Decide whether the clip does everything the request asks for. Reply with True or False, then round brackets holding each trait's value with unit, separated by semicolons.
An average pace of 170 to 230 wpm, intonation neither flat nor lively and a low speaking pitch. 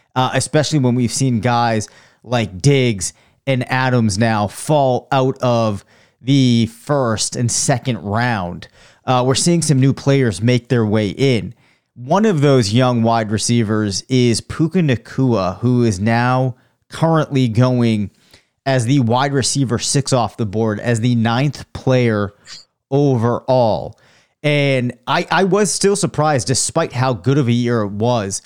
False (150 wpm; 3.0 semitones; 125 Hz)